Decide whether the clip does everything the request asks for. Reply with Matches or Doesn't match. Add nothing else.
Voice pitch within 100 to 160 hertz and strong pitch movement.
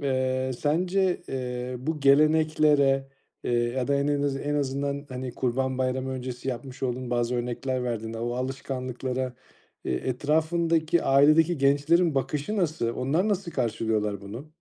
Doesn't match